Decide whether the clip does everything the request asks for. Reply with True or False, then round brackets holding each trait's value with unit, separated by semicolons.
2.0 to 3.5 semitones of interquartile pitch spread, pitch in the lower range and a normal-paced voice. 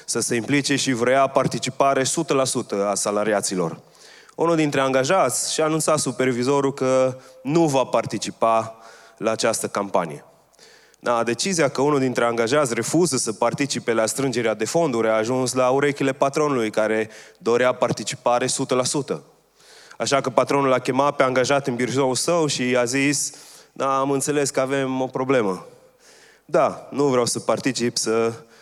True (3.0 semitones; 130 Hz; 145 wpm)